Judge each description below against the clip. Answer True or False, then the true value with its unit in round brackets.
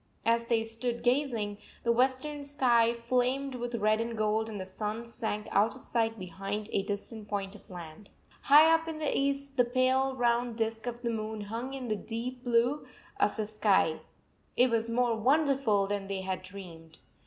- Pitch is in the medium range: False (230 Hz)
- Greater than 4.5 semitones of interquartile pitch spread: False (3.3 semitones)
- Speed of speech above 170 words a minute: True (190 wpm)